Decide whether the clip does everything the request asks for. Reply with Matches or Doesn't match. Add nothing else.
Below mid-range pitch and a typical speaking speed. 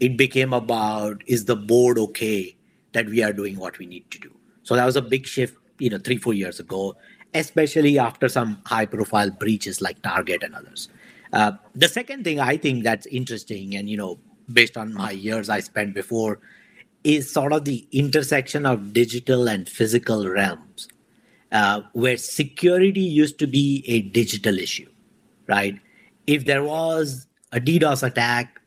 Matches